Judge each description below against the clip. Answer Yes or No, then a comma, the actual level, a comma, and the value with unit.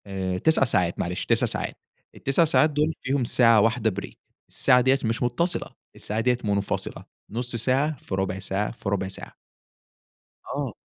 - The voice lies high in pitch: No, low, 115 Hz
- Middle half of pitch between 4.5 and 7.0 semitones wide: Yes, average, 4.8 semitones